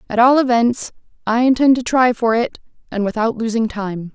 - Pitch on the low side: No, high, 235 Hz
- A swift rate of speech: No, average, 190 wpm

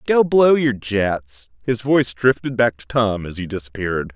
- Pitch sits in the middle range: No, low, 115 Hz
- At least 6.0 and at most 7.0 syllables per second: No, 4.6 syllables/s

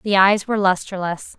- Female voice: Yes, female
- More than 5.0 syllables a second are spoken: Yes, 5.4 syllables/s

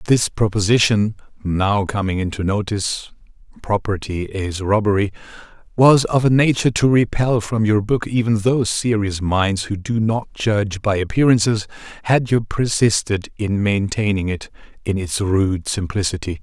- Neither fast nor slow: No, slow, 130 wpm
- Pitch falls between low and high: No, low, 105 Hz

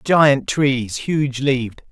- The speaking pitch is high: No, low, 135 Hz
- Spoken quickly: No, slow, 125 wpm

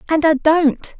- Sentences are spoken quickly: No, average, 180 wpm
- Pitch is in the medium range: No, very high, 310 Hz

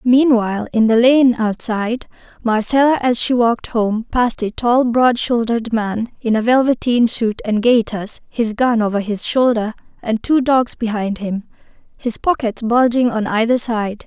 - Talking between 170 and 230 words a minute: No, average, 160 wpm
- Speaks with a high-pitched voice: Yes, high, 230 Hz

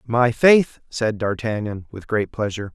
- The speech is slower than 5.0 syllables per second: Yes, 4.4 syllables/s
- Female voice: No, male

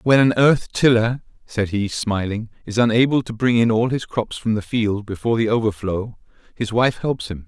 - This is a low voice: Yes, low, 115 Hz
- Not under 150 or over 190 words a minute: No, average, 200 wpm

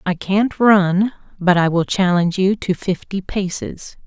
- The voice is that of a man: No, female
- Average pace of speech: Yes, average, 160 wpm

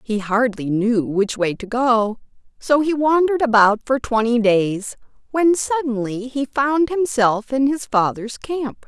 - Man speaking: No, female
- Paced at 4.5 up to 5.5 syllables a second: No, 4.0 syllables/s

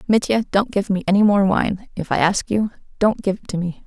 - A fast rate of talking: Yes, fast, 235 wpm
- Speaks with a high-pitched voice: Yes, high, 200 Hz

